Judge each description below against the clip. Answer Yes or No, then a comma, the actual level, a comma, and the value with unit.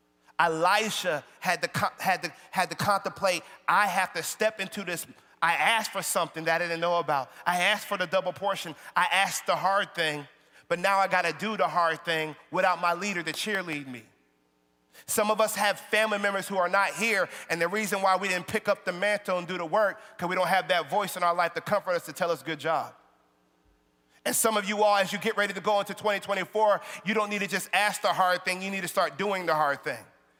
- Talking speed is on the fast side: Yes, fast, 235 wpm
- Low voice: No, medium, 185 Hz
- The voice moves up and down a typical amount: Yes, average, 3.3 semitones